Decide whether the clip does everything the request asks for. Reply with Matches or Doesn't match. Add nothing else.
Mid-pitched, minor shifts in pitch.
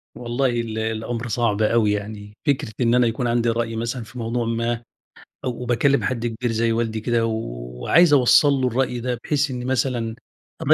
Doesn't match